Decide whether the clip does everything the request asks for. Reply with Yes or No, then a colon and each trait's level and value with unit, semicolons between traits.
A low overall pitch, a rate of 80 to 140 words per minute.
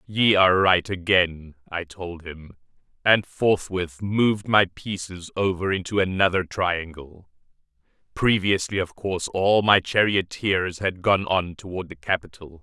Yes: very low, 90 Hz; slow, 135 wpm